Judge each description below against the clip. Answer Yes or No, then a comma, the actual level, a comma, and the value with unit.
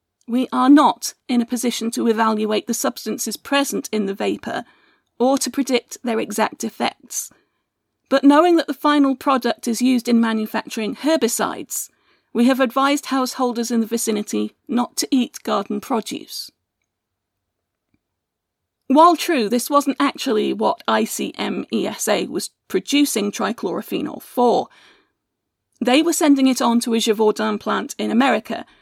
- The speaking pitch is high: Yes, high, 240 Hz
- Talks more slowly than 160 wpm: Yes, slow, 135 wpm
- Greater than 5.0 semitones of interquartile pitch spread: No, average, 4.0 semitones